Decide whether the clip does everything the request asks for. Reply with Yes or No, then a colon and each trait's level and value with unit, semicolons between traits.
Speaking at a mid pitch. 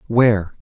No: low, 110 Hz